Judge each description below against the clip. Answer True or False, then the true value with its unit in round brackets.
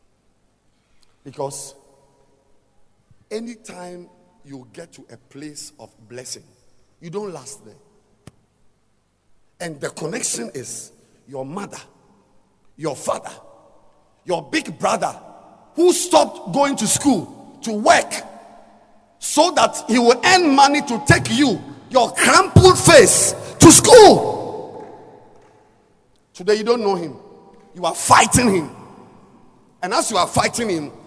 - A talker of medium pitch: True (180 Hz)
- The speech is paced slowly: True (115 wpm)